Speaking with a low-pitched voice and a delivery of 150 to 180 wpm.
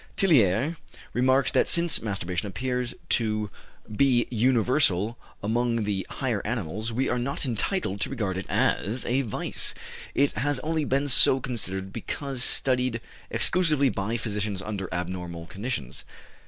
No: low, 120 Hz; average, 140 wpm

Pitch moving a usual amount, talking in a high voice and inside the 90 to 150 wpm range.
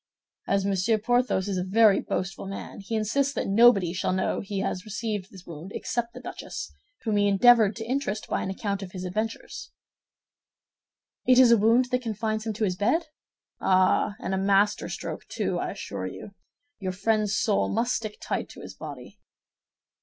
No: average, 3.0 semitones; high, 210 Hz; average, 185 wpm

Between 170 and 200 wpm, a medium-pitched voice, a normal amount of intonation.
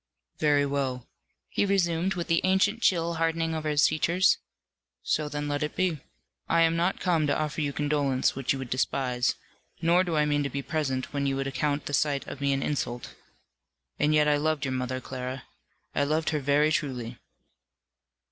Yes: average, 190 wpm; medium, 150 Hz; average, 3.1 semitones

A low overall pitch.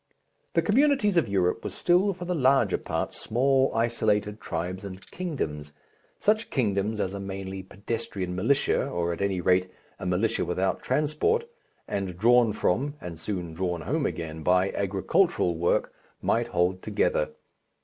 Yes: low, 100 Hz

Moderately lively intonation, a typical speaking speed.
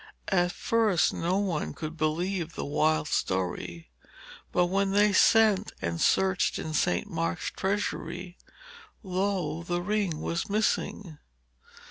No: average, 3.9 semitones; slow, 120 wpm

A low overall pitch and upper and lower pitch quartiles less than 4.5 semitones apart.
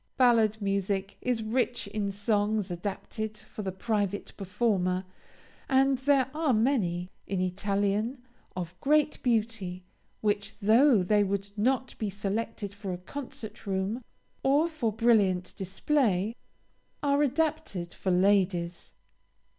No: high, 210 Hz; average, 4.0 semitones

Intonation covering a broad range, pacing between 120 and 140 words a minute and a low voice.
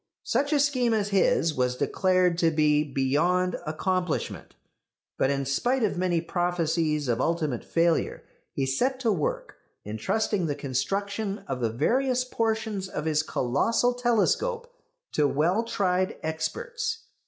No: wide, 6.7 semitones; slow, 135 wpm; medium, 180 Hz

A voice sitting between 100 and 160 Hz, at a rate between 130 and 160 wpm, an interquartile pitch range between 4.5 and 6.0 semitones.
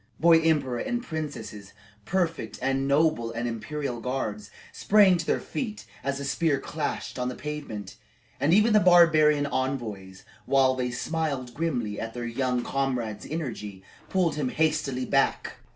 Yes: low, 135 Hz; average, 150 wpm; average, 4.8 semitones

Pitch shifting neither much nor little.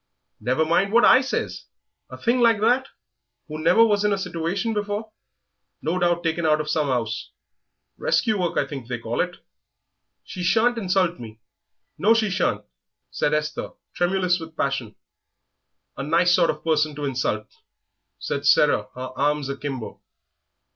No: wide, 5.9 semitones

